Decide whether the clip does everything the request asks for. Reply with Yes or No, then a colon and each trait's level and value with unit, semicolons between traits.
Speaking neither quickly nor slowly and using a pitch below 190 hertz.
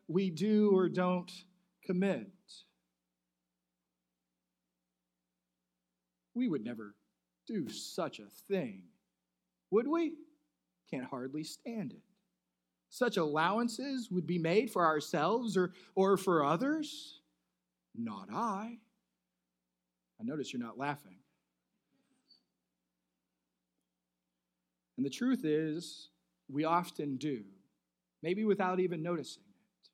No: slow, 95 wpm; medium, 140 Hz